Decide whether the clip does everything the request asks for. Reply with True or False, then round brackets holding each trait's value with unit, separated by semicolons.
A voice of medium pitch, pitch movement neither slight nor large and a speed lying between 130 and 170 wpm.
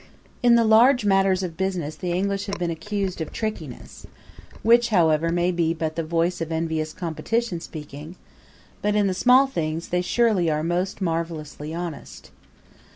True (175 Hz; 3.8 semitones; 160 wpm)